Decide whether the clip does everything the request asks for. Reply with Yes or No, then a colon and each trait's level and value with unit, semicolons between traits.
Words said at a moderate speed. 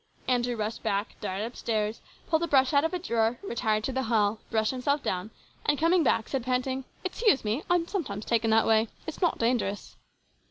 No: fast, 210 wpm